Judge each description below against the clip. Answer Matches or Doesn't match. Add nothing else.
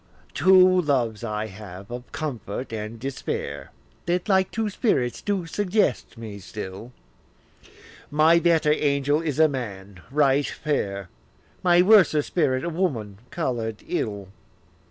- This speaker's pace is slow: Matches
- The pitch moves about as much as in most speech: Doesn't match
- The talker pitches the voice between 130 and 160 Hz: Matches